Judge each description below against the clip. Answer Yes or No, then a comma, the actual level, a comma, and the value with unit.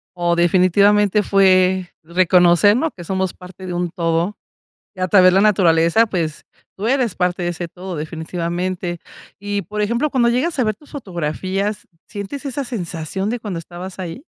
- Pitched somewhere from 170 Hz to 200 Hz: Yes, medium, 185 Hz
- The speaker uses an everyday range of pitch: Yes, average, 3.2 semitones